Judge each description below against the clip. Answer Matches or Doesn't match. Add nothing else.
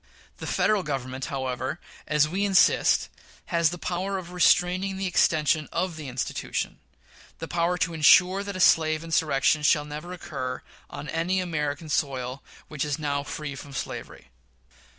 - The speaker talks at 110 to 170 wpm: Matches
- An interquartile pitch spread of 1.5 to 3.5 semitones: Doesn't match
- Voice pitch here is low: Doesn't match